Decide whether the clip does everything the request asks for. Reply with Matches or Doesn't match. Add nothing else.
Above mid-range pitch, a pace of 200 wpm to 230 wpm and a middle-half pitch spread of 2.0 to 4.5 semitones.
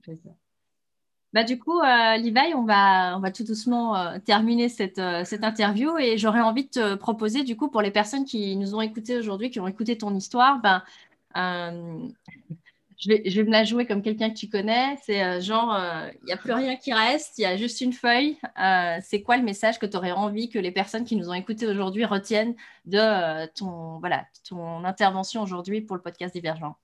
Matches